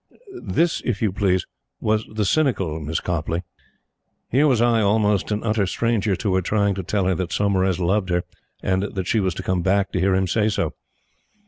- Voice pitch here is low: Yes, low, 100 Hz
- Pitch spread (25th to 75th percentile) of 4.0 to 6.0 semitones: No, average, 2.8 semitones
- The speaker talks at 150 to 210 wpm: Yes, average, 195 wpm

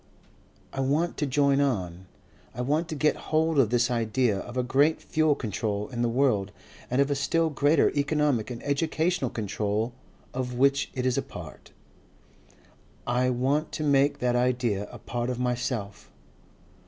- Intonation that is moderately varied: Yes, average, 3.2 semitones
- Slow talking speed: No, average, 165 wpm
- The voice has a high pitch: No, low, 130 Hz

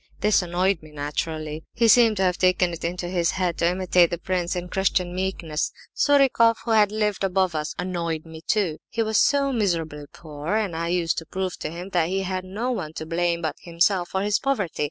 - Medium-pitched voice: Yes, medium, 180 Hz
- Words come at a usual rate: No, fast, 210 wpm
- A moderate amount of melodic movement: Yes, average, 3.1 semitones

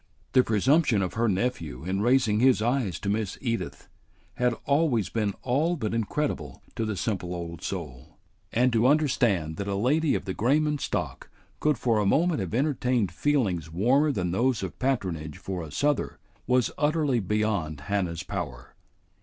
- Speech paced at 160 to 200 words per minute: Yes, average, 165 wpm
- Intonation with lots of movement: Yes, wide, 6.1 semitones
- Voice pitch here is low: Yes, low, 110 Hz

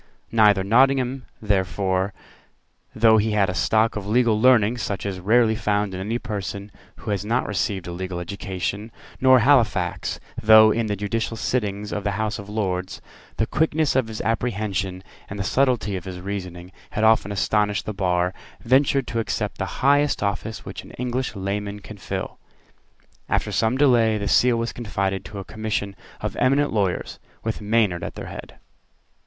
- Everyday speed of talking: Yes, average, 170 wpm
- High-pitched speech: No, low, 105 Hz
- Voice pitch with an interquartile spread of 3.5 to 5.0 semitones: No, average, 2.9 semitones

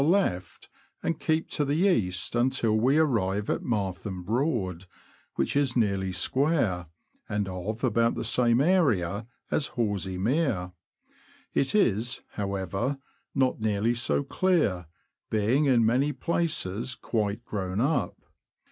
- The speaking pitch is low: Yes, low, 115 Hz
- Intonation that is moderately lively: No, wide, 6.2 semitones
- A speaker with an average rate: No, slow, 130 wpm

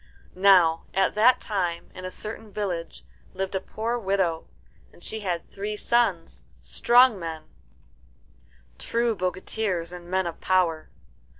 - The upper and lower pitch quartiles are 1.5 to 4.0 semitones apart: Yes, average, 3.6 semitones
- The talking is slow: Yes, slow, 130 wpm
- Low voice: No, high, 190 Hz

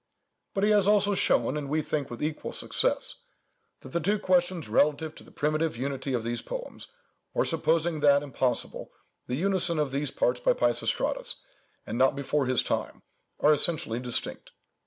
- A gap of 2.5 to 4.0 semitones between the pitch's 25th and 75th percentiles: No, average, 4.7 semitones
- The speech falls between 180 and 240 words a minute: No, average, 170 wpm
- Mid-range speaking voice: Yes, medium, 150 Hz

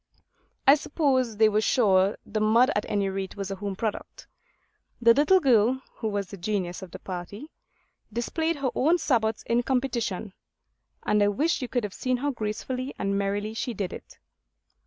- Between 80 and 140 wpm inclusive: No, average, 180 wpm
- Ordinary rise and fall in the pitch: Yes, average, 4.3 semitones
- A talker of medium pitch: No, high, 220 Hz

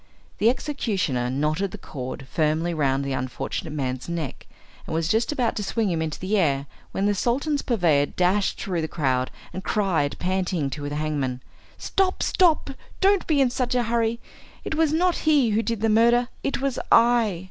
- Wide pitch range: Yes, wide, 8.1 semitones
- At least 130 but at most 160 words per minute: No, average, 185 wpm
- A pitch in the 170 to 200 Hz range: Yes, high, 190 Hz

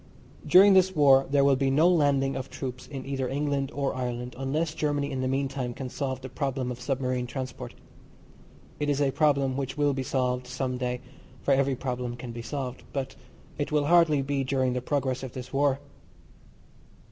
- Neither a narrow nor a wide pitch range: No, narrow, 1.9 semitones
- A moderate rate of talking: Yes, average, 190 wpm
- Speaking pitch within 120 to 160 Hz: Yes, low, 135 Hz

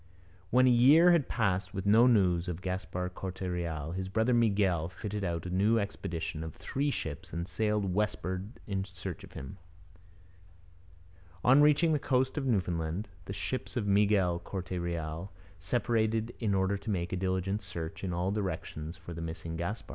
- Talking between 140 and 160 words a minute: No, average, 170 wpm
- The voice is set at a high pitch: No, very low, 95 Hz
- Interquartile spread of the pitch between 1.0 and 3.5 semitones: No, average, 4.0 semitones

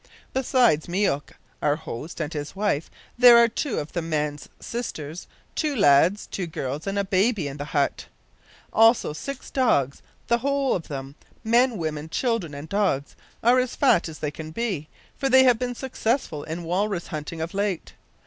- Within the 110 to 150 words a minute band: No, average, 175 wpm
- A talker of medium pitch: Yes, medium, 180 Hz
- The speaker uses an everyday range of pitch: No, wide, 7.7 semitones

